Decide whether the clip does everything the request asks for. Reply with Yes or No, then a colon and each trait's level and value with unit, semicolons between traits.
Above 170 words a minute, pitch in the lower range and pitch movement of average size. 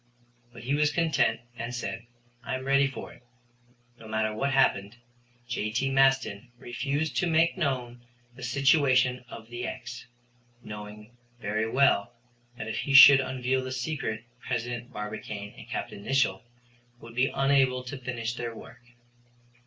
No: average, 145 wpm; low, 125 Hz; average, 3.0 semitones